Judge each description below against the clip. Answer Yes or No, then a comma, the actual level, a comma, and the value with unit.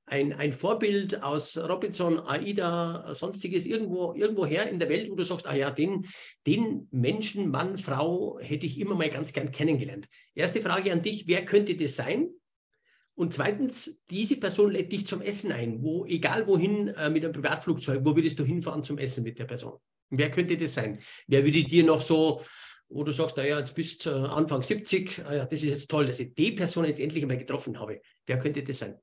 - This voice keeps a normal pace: No, fast, 205 wpm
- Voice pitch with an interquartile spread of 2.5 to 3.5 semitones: No, average, 4.4 semitones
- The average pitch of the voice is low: No, medium, 160 Hz